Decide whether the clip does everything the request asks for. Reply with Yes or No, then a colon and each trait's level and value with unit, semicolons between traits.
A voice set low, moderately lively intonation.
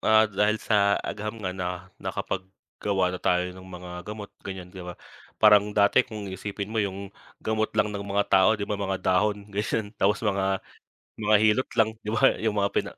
No: low, 100 Hz; narrow, 2.1 semitones